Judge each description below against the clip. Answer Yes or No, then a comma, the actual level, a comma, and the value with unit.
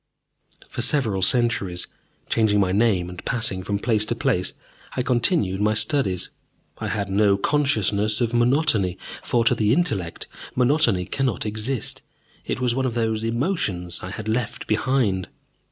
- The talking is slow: No, average, 150 wpm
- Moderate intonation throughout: Yes, average, 4.1 semitones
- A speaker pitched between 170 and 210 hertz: No, low, 110 Hz